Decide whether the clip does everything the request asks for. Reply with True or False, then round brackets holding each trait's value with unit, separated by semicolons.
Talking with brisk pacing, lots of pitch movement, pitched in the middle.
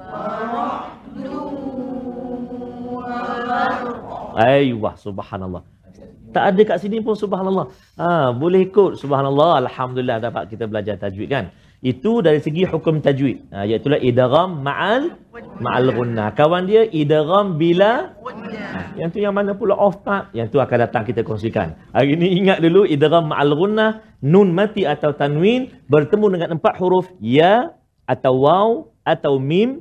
True (130 wpm; 8.7 semitones; 170 Hz)